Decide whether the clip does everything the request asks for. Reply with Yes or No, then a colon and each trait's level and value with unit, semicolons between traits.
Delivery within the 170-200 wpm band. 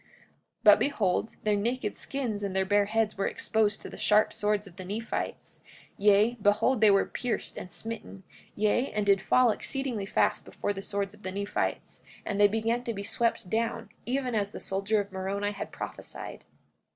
Yes: average, 190 wpm